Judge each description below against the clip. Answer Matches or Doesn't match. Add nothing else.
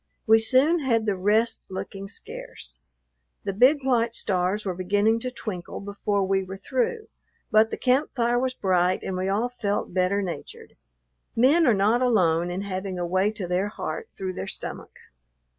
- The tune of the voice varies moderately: Matches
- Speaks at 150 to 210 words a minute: Matches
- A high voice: Matches